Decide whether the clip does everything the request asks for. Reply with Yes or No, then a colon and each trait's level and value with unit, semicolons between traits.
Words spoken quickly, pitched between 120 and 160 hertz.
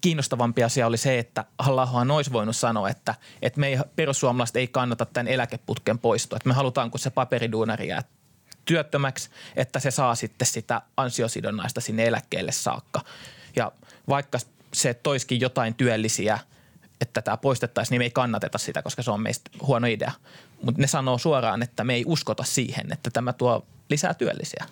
Yes: fast, 170 wpm; low, 125 Hz